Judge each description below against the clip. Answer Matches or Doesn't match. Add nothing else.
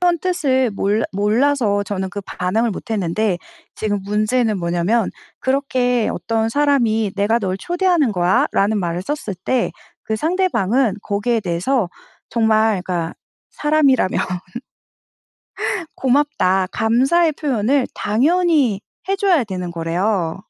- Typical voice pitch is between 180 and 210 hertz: Doesn't match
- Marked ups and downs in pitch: Matches